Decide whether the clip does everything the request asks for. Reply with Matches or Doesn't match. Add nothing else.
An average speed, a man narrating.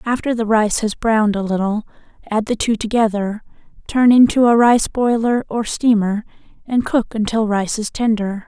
Doesn't match